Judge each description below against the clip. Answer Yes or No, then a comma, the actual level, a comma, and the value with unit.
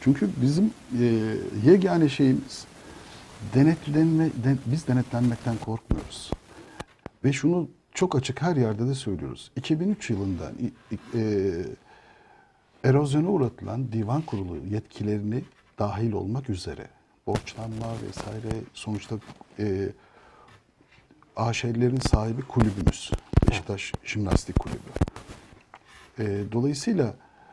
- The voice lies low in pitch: Yes, low, 115 Hz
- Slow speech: Yes, slow, 90 wpm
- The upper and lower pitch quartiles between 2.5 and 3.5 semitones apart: No, average, 4.3 semitones